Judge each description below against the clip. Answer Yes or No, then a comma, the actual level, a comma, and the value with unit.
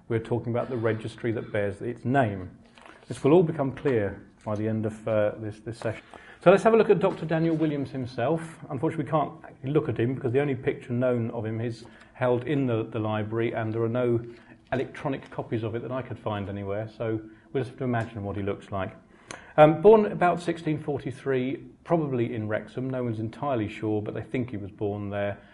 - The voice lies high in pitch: No, low, 120 Hz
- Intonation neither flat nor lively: Yes, average, 4.2 semitones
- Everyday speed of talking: No, fast, 220 wpm